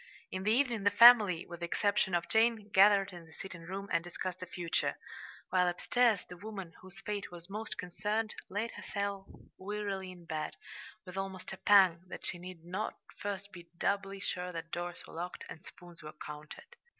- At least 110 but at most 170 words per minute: No, average, 190 wpm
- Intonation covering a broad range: No, average, 2.8 semitones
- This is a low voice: No, high, 190 Hz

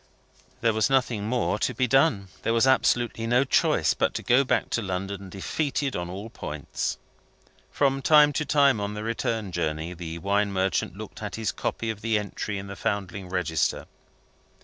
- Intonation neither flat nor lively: Yes, average, 4.5 semitones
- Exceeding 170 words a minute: Yes, average, 180 wpm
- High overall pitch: No, low, 105 Hz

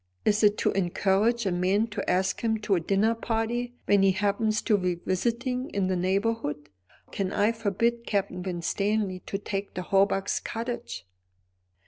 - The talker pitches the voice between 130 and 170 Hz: No, high, 200 Hz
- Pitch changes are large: No, average, 3.1 semitones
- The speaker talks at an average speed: Yes, average, 160 wpm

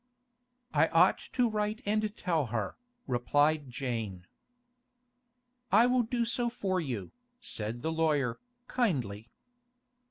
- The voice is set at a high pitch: No, medium, 160 Hz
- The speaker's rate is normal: No, slow, 115 wpm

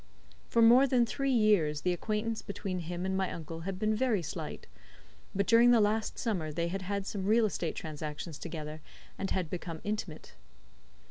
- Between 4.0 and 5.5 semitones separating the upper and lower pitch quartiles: Yes, average, 4.5 semitones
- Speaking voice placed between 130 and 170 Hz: No, high, 190 Hz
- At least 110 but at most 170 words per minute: No, average, 180 wpm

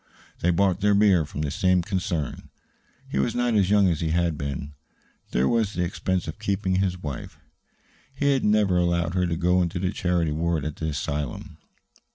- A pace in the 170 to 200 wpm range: Yes, average, 195 wpm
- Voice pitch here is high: No, very low, 90 Hz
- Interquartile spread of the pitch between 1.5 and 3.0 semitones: No, average, 3.5 semitones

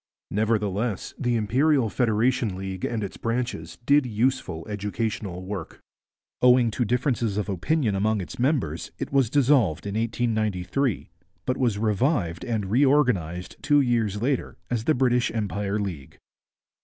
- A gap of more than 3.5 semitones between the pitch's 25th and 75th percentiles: Yes, average, 4.0 semitones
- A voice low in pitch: Yes, low, 110 Hz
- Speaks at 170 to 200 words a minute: No, slow, 135 wpm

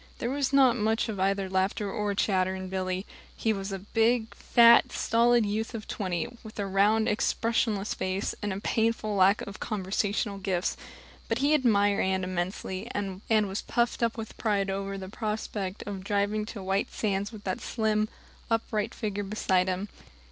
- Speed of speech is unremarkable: Yes, average, 170 wpm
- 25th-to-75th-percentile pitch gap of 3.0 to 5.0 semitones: No, narrow, 2.4 semitones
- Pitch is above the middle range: Yes, high, 205 Hz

